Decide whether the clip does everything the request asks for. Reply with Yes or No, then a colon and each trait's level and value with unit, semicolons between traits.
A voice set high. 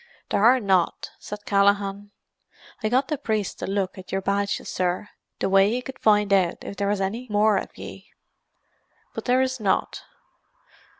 Yes: high, 205 Hz